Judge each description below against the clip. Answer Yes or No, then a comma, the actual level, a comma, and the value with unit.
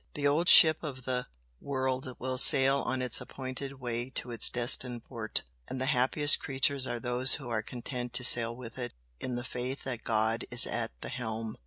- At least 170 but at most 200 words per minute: Yes, average, 195 wpm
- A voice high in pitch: No, low, 125 Hz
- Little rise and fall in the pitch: Yes, narrow, 1.6 semitones